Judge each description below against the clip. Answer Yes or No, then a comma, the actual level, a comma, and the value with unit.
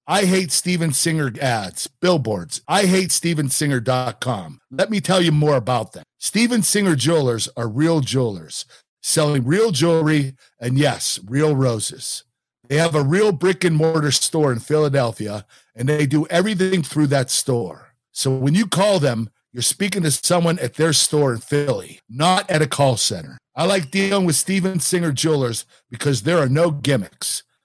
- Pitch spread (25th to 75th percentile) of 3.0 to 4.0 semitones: No, average, 4.9 semitones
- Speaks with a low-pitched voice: No, medium, 150 Hz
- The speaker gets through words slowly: No, average, 165 wpm